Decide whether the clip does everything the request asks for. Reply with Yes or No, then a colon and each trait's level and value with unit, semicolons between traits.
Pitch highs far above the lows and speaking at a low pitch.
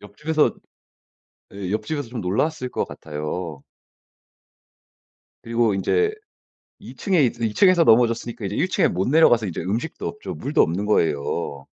Yes: wide, 8.3 semitones; low, 115 Hz